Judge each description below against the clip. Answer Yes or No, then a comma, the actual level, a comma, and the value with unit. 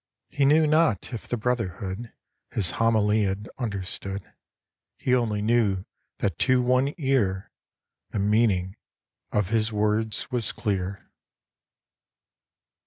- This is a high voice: No, low, 110 Hz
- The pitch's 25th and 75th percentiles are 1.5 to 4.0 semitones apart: Yes, average, 3.7 semitones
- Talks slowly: Yes, slow, 110 wpm